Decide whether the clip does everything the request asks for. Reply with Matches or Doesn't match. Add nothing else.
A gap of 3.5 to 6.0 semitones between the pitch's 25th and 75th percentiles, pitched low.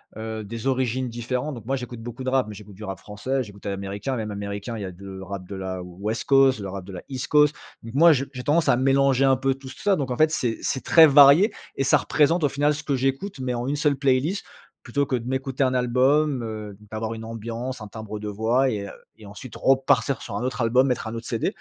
Matches